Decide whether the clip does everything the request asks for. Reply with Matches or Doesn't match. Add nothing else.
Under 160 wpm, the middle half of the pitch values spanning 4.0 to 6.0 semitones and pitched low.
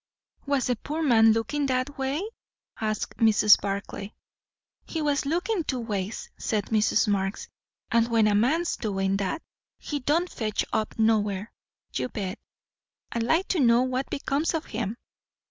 Doesn't match